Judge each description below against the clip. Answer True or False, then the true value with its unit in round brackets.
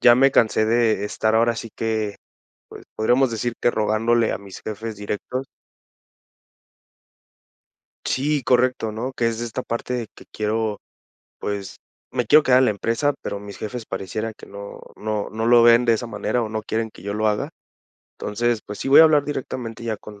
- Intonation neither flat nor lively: False (2.2 semitones)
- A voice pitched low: True (115 Hz)